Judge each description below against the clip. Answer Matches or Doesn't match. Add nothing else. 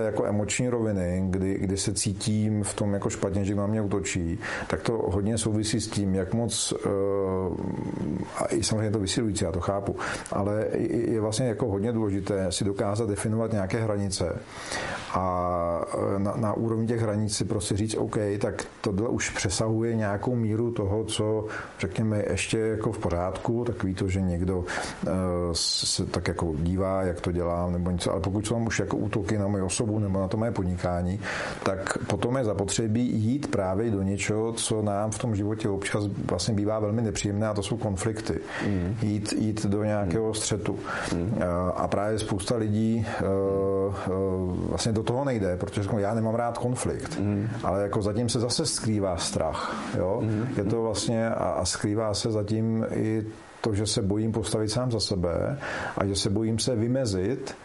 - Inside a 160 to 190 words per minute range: Matches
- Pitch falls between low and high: Doesn't match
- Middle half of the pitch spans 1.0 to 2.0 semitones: Doesn't match